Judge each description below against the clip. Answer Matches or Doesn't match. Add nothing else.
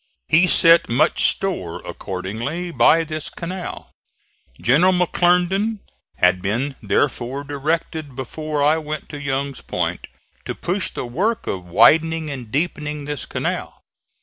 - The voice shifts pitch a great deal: Doesn't match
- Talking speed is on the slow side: Matches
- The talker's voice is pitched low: Doesn't match